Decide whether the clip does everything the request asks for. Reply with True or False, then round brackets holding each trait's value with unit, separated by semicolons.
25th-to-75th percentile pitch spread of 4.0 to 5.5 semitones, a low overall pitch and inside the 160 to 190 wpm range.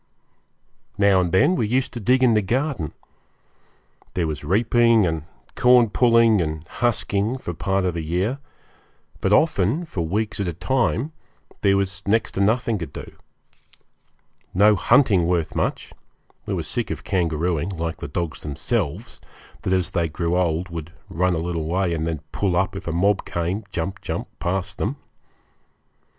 True (4.7 semitones; 95 Hz; 165 wpm)